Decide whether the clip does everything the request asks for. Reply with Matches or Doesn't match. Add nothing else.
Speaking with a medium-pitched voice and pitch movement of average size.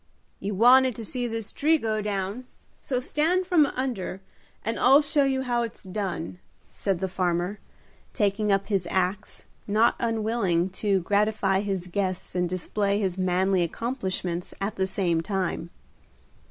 Doesn't match